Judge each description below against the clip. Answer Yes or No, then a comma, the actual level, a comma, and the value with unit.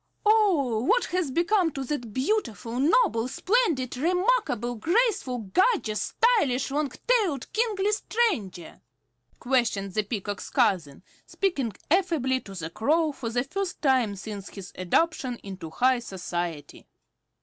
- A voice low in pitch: No, very high, 260 Hz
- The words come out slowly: Yes, slow, 125 wpm